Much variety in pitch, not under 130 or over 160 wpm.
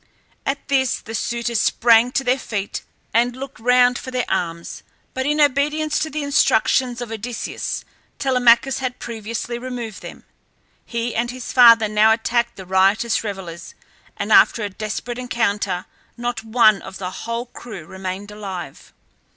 No: average, 3.0 semitones; average, 150 wpm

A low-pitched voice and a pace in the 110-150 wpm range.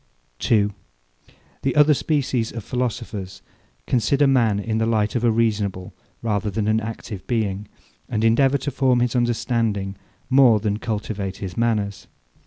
Yes: low, 115 Hz; average, 145 wpm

